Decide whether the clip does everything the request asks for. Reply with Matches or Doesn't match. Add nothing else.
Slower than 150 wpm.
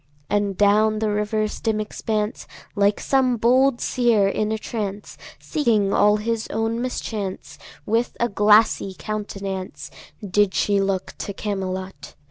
Matches